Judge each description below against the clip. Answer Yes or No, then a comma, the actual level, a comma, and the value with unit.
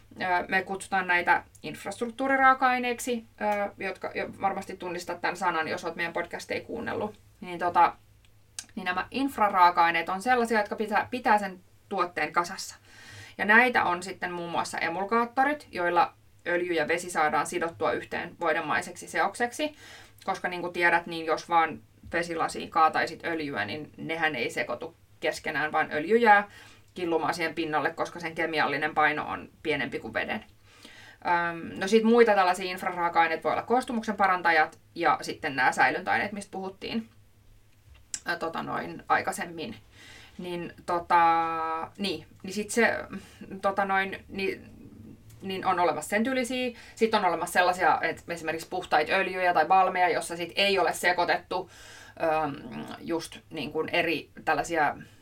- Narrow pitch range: No, average, 3.8 semitones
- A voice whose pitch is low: No, medium, 175 Hz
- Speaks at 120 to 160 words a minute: Yes, average, 140 wpm